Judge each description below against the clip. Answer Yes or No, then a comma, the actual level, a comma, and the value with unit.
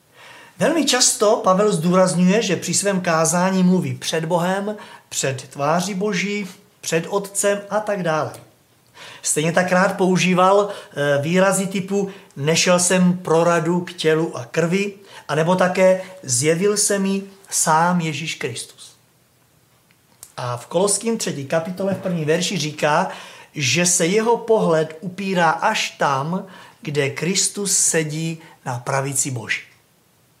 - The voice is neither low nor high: Yes, medium, 180 Hz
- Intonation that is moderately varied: Yes, average, 3.6 semitones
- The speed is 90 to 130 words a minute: Yes, average, 120 wpm